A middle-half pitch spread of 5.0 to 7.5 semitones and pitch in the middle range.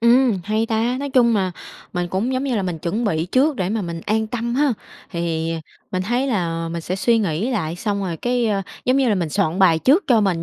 No: wide, 5.6 semitones; high, 210 Hz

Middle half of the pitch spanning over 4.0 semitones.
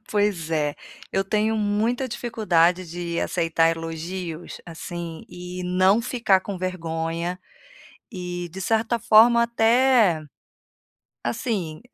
Yes: average, 4.6 semitones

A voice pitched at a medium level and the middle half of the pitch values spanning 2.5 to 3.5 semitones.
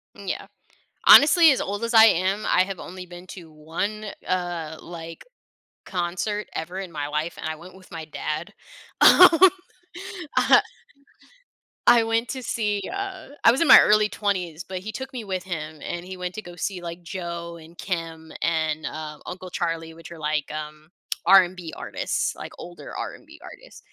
No: medium, 175 Hz; average, 3.9 semitones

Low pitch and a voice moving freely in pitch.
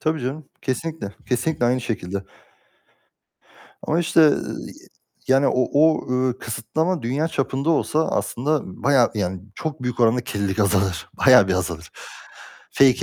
Yes: low, 125 Hz; wide, 6.6 semitones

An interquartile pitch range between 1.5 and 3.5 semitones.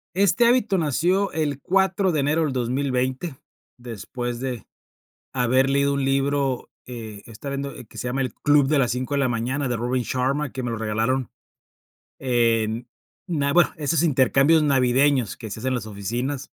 Yes: average, 3.0 semitones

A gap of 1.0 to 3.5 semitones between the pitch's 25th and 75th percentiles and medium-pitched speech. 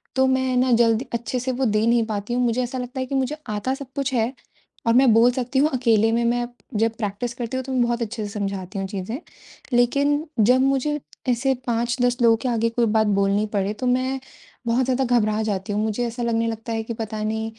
No: average, 2.7 semitones; high, 235 Hz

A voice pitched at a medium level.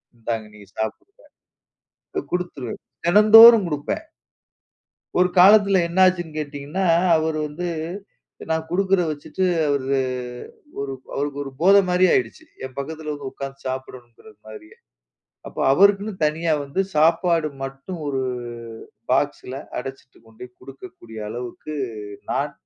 Yes: medium, 155 Hz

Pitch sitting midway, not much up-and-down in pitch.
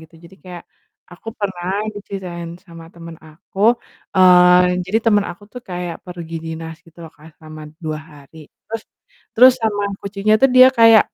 No: medium, 180 Hz; average, 3.6 semitones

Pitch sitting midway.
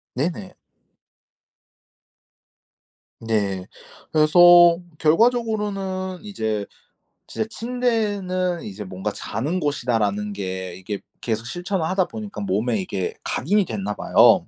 Yes: medium, 155 Hz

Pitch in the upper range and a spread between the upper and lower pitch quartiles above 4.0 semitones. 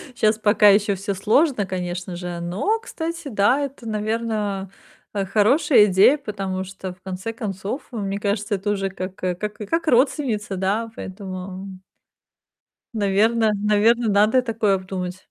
No: high, 205 Hz; average, 3.0 semitones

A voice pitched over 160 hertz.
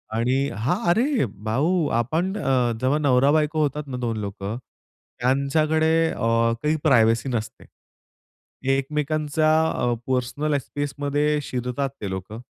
No: low, 135 Hz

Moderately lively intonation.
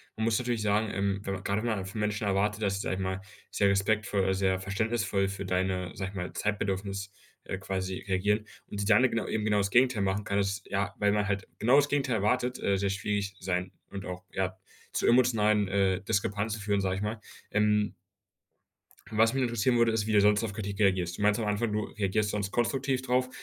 No: narrow, 1.9 semitones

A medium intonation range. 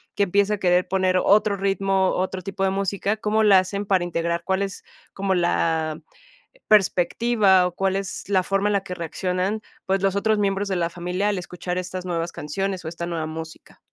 No: narrow, 1.9 semitones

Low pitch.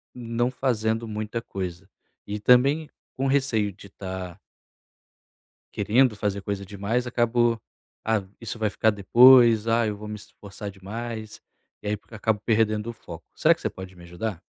Yes: low, 110 Hz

